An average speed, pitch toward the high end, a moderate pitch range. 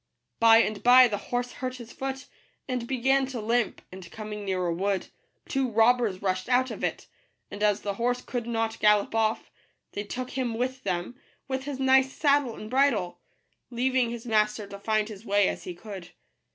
Yes: average, 190 wpm; high, 230 Hz; average, 3.7 semitones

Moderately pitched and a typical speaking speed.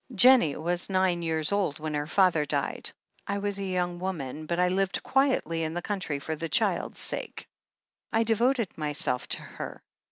Yes: medium, 175 Hz; average, 185 wpm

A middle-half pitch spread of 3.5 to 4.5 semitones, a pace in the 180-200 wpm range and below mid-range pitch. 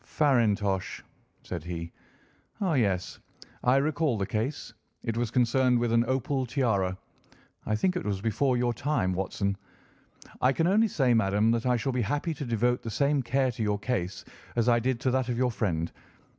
Yes: average, 4.1 semitones; average, 185 wpm; low, 120 Hz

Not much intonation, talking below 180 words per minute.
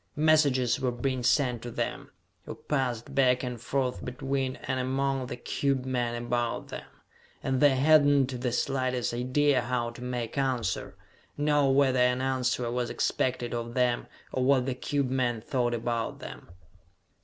Yes: narrow, 1.8 semitones; average, 155 wpm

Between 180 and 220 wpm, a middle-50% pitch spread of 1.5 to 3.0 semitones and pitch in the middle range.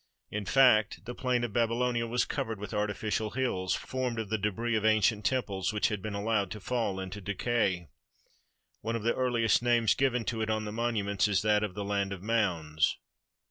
No: average, 195 wpm; average, 2.7 semitones; low, 110 Hz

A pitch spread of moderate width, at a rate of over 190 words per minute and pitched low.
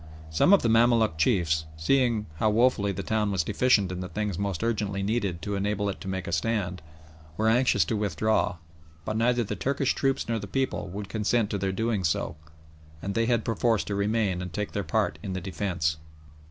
Yes: average, 3.4 semitones; fast, 205 wpm; low, 105 Hz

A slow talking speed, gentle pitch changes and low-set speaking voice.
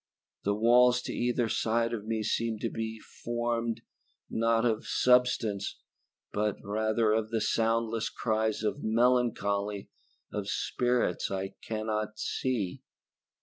Yes: slow, 120 wpm; narrow, 1.6 semitones; low, 115 Hz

